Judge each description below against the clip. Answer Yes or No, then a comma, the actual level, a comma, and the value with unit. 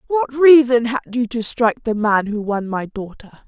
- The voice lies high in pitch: Yes, high, 235 Hz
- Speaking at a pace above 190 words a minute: Yes, fast, 205 wpm